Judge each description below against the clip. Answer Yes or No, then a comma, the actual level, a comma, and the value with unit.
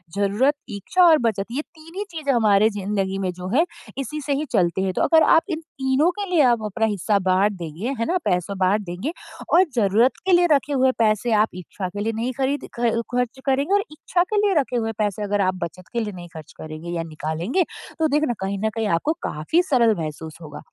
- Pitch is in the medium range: No, high, 220 Hz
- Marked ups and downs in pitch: Yes, wide, 7.3 semitones